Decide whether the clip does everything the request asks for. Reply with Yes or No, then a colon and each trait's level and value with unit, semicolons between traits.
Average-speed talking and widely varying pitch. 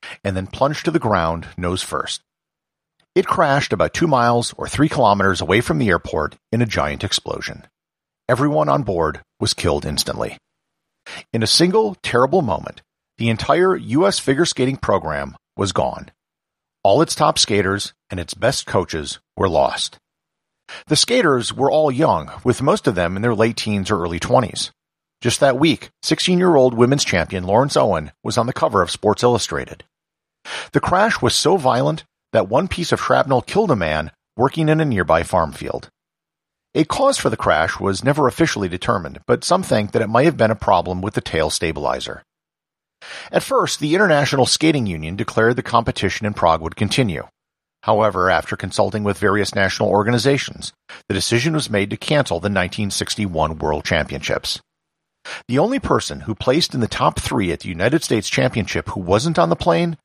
Yes: average, 175 wpm; wide, 6.1 semitones